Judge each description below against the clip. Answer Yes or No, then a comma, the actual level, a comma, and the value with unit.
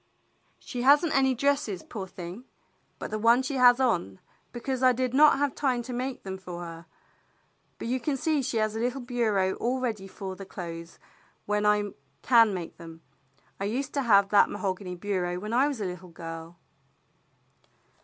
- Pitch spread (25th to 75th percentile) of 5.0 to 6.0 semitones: Yes, wide, 5.5 semitones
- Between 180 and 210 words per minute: Yes, average, 185 wpm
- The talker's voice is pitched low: No, high, 215 Hz